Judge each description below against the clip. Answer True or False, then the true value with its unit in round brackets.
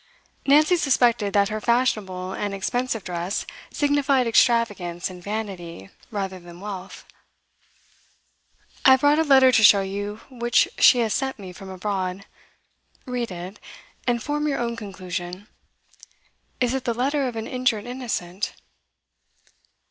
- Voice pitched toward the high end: True (215 Hz)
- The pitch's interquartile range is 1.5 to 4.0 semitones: False (5.0 semitones)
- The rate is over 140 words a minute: False (135 wpm)